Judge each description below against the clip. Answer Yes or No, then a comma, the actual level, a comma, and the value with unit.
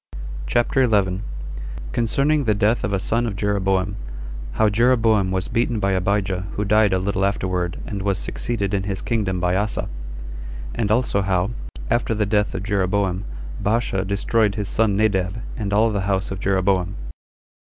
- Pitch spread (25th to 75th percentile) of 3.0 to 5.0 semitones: No, narrow, 2.4 semitones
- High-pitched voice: No, low, 100 Hz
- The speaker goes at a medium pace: Yes, average, 160 wpm